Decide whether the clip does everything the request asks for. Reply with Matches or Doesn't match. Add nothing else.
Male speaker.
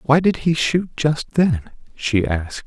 Matches